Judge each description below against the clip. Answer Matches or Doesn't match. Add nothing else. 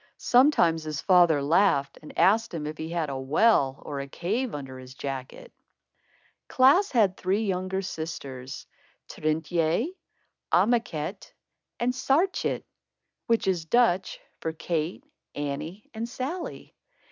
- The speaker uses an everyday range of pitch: Doesn't match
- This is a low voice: Doesn't match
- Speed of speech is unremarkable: Doesn't match